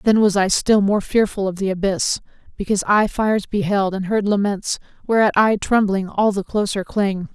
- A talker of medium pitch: No, high, 200 Hz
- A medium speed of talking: Yes, average, 190 wpm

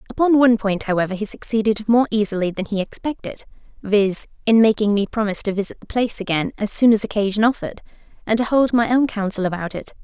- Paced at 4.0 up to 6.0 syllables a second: No, 6.4 syllables/s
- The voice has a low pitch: No, high, 215 Hz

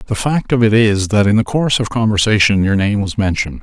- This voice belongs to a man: Yes, male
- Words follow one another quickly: Yes, fast, 250 wpm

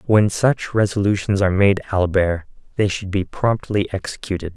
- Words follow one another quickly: No, average, 145 wpm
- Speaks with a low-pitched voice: Yes, low, 100 Hz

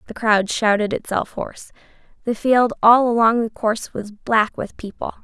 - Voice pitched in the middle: No, high, 225 Hz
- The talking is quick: No, average, 170 wpm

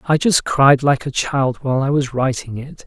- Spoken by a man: Yes, male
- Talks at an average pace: No, fast, 230 wpm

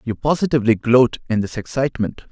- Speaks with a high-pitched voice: No, low, 120 Hz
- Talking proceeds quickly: No, average, 155 wpm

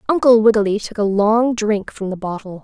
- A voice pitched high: Yes, high, 215 Hz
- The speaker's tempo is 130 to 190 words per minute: No, fast, 205 wpm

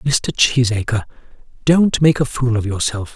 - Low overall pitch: Yes, low, 120 Hz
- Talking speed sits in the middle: Yes, average, 150 wpm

